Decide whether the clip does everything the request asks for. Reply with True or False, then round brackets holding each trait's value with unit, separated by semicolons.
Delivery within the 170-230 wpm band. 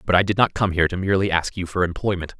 False (300 wpm)